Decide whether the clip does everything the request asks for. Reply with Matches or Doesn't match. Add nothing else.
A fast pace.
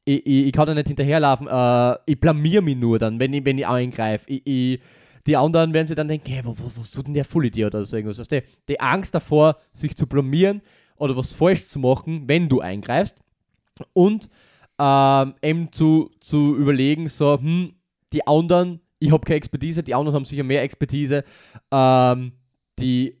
Matches